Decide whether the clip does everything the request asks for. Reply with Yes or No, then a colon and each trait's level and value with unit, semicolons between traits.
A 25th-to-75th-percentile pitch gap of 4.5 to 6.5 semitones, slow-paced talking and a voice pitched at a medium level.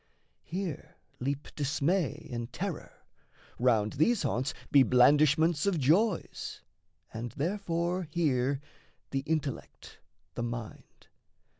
Yes: average, 4.9 semitones; slow, 100 wpm; medium, 145 Hz